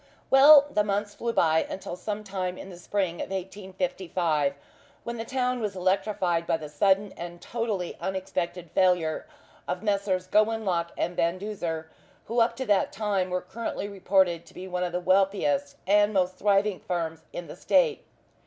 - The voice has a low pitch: No, high, 190 Hz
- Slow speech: No, average, 170 wpm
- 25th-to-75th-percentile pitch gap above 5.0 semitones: No, average, 2.9 semitones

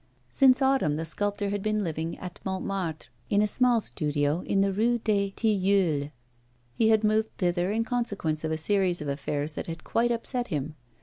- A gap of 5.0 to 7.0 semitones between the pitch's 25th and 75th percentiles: Yes, wide, 5.4 semitones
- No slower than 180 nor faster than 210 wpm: Yes, average, 185 wpm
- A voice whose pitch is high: Yes, high, 195 Hz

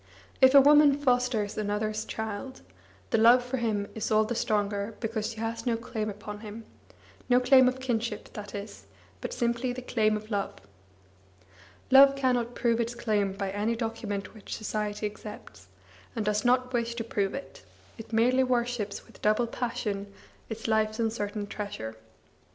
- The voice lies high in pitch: Yes, high, 225 Hz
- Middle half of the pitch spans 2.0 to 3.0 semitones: Yes, average, 2.7 semitones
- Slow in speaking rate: No, average, 160 wpm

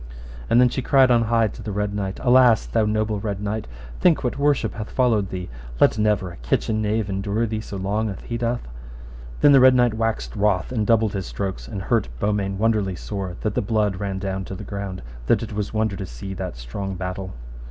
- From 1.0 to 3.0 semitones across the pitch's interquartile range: Yes, narrow, 2.6 semitones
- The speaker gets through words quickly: Yes, fast, 220 wpm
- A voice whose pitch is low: Yes, low, 105 Hz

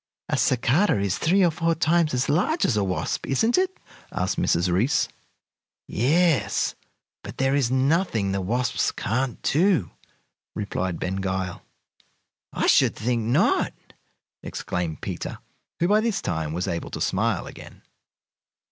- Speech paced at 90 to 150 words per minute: Yes, average, 140 wpm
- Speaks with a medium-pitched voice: No, low, 125 Hz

